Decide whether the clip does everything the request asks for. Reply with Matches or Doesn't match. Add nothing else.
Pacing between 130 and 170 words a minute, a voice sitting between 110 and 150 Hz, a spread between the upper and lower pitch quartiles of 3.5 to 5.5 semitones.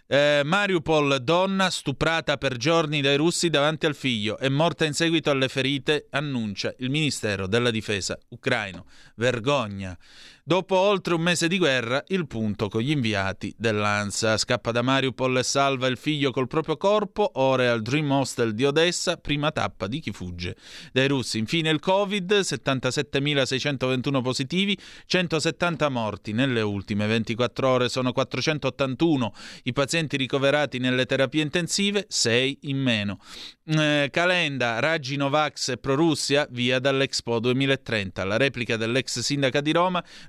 Matches